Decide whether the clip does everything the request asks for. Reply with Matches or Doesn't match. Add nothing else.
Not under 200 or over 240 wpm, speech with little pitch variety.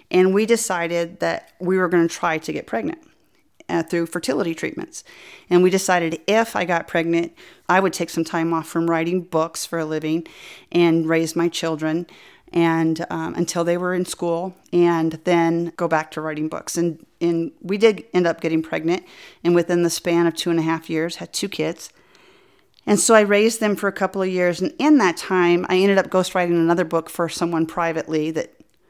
Matches